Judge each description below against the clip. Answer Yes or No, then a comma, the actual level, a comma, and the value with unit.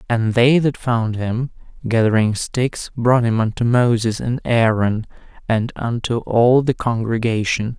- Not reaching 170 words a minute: Yes, average, 140 wpm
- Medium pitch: No, low, 115 Hz